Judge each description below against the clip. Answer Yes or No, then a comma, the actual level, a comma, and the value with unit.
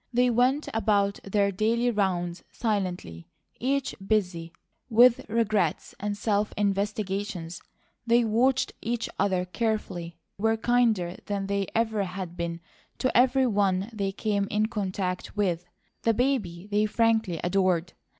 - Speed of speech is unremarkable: No, slow, 125 wpm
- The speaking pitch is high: Yes, high, 205 Hz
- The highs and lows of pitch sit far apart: No, average, 3.5 semitones